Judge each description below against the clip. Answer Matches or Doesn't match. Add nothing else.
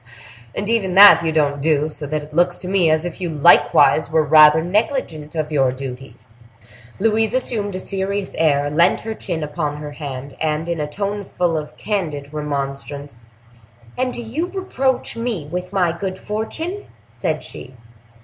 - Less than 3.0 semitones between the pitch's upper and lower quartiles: Doesn't match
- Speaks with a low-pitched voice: Doesn't match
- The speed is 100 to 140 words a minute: Doesn't match